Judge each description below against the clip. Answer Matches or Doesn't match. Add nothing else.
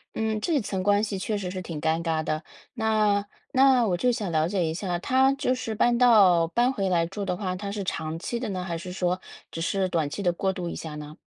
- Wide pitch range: Doesn't match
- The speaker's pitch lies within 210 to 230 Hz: Doesn't match